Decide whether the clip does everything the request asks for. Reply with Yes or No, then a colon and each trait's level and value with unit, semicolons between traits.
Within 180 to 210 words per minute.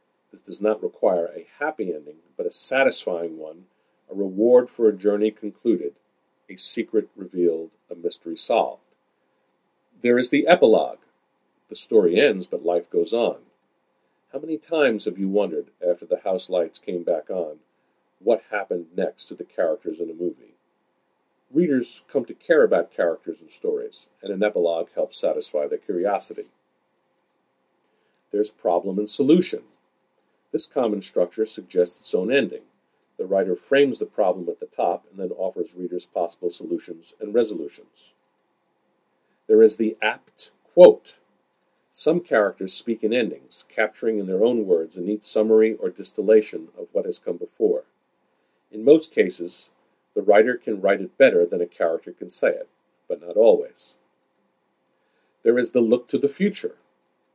No: average, 155 wpm